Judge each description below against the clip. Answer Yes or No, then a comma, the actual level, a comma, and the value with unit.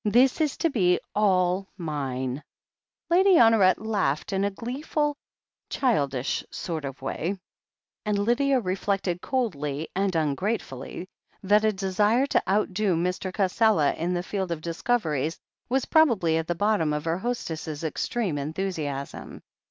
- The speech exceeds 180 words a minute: No, slow, 135 wpm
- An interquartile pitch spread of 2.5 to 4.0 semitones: No, wide, 5.4 semitones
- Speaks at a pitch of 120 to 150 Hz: No, high, 190 Hz